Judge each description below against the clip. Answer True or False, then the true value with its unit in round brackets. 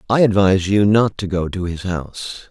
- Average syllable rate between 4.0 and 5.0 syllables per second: False (5.4 syllables/s)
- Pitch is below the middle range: True (95 Hz)